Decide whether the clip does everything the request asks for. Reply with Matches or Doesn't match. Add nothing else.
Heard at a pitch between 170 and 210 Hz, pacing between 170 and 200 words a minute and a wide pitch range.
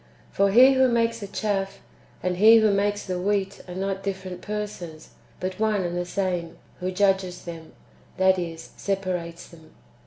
Doesn't match